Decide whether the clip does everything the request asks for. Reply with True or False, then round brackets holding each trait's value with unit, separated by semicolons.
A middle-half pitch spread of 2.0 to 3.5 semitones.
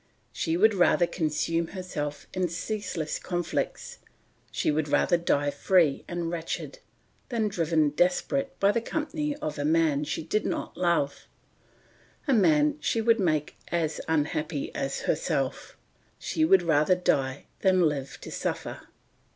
False (4.2 semitones)